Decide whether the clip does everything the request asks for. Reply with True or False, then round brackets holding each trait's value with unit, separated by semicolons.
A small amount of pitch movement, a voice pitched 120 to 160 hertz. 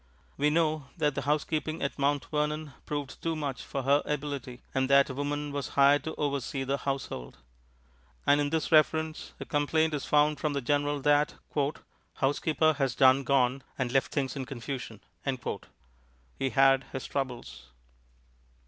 True (1.7 semitones; 140 Hz)